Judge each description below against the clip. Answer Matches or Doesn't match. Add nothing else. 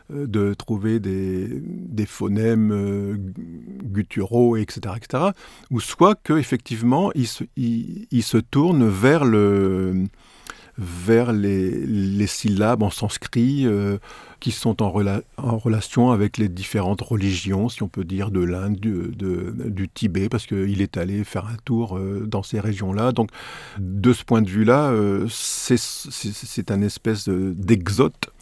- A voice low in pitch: Matches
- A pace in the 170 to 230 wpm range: Doesn't match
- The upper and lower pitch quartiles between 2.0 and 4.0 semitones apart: Matches